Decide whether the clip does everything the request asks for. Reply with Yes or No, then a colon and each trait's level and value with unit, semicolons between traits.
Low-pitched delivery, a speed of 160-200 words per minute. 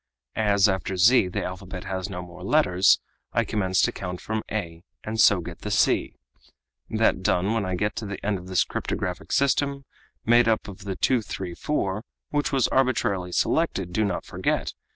Yes: low, 100 Hz; average, 175 wpm